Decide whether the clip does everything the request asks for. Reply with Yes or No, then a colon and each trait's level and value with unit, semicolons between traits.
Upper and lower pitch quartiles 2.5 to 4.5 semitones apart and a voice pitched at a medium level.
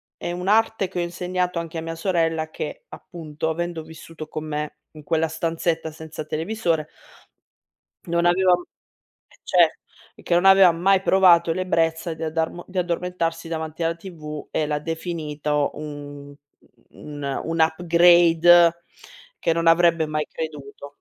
No: narrow, 1.9 semitones; medium, 165 Hz